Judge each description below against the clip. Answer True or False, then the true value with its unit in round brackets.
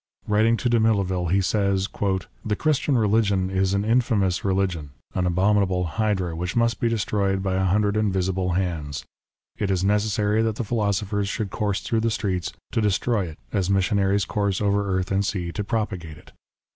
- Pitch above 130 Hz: False (100 Hz)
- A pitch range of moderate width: False (2.3 semitones)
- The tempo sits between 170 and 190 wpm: True (175 wpm)